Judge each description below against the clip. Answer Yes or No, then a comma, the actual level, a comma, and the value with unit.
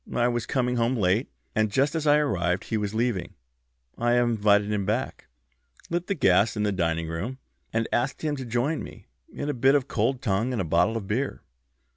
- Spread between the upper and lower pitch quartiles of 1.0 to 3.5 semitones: No, average, 4.3 semitones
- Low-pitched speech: Yes, low, 115 Hz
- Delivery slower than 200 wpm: No, fast, 205 wpm